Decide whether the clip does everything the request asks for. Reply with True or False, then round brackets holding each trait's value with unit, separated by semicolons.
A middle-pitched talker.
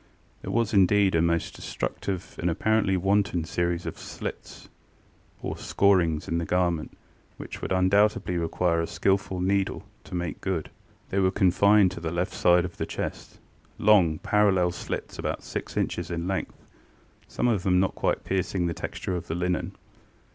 False (90 Hz)